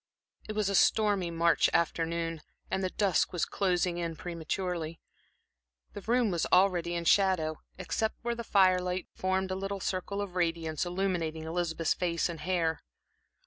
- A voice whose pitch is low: No, medium, 180 Hz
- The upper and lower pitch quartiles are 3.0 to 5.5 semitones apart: No, narrow, 2.4 semitones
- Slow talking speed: No, average, 150 wpm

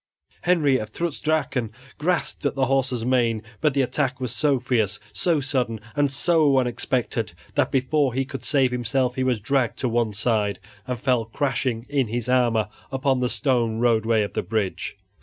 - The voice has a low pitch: Yes, low, 125 Hz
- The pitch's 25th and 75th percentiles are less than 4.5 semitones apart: Yes, average, 3.1 semitones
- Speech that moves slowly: No, average, 175 wpm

